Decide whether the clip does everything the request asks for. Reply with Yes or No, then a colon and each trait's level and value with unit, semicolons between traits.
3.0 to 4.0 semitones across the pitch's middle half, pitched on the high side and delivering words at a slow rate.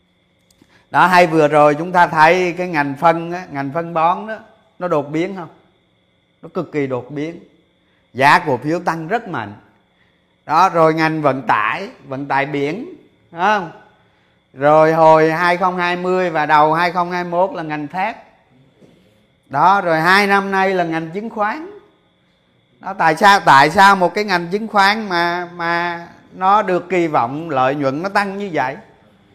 No: average, 3.7 semitones; medium, 170 Hz; slow, 160 wpm